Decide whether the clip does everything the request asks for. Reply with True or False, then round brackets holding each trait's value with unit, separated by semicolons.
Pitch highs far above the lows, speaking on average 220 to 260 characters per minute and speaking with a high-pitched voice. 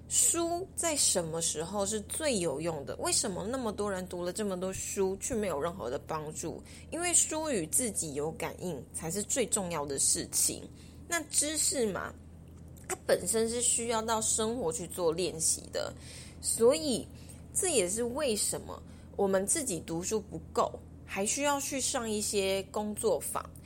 True (7.5 semitones; 235 characters per minute; 220 Hz)